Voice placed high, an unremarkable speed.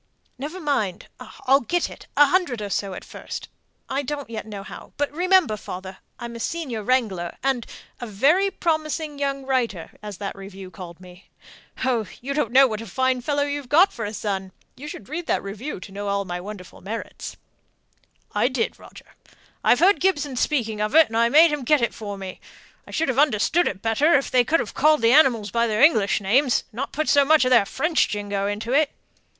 No: high, 245 Hz; fast, 210 wpm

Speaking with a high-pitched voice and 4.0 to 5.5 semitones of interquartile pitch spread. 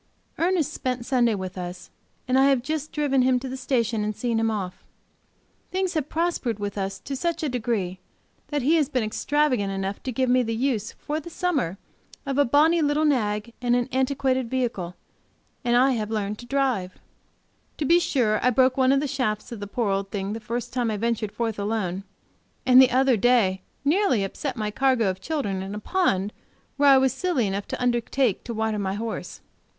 Yes: high, 245 Hz; average, 4.5 semitones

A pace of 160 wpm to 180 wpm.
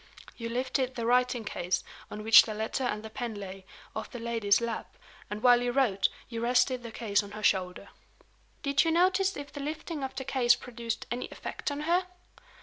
No: average, 200 wpm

